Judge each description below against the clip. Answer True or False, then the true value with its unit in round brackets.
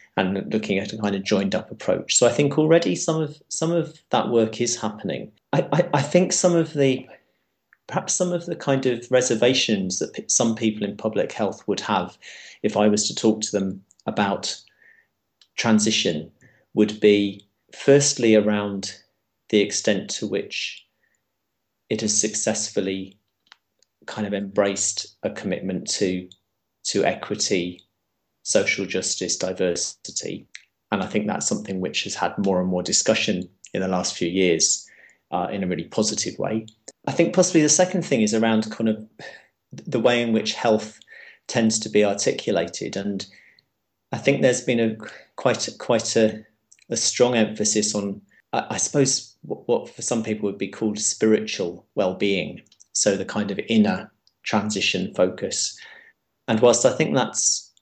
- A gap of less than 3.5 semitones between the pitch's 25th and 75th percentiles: False (4.0 semitones)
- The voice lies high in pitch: False (110 Hz)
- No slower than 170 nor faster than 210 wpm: False (160 wpm)